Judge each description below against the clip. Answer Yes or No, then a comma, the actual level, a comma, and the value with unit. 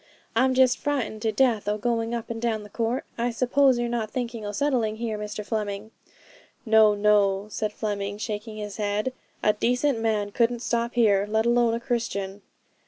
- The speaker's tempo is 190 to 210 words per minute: No, average, 180 wpm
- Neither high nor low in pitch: No, high, 225 Hz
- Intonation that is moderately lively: No, narrow, 2.3 semitones